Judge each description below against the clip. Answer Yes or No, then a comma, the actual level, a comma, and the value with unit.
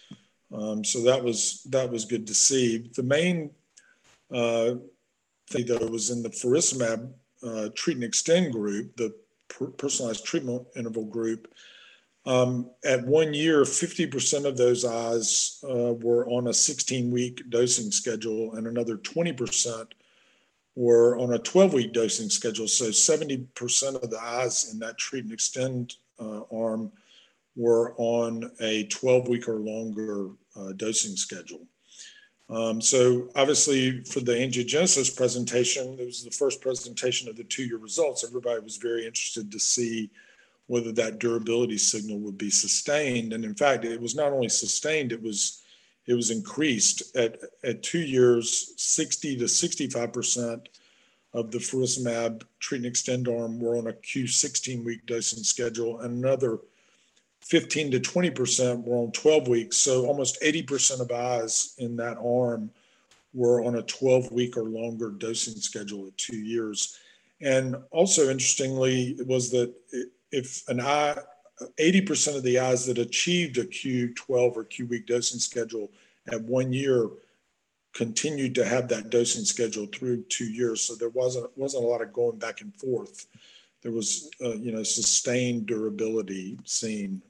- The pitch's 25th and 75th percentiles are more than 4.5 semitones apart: No, narrow, 2.5 semitones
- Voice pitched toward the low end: Yes, low, 120 Hz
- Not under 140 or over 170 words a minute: Yes, average, 155 wpm